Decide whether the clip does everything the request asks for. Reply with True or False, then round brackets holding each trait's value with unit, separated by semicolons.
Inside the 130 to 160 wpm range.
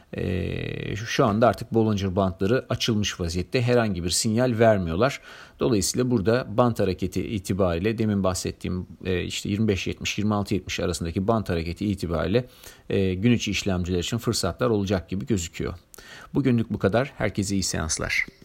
True (135 wpm)